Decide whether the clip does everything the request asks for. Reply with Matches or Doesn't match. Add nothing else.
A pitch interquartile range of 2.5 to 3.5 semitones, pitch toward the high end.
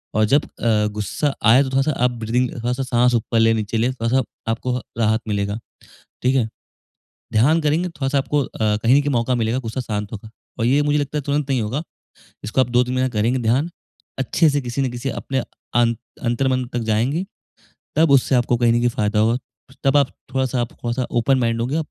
Doesn't match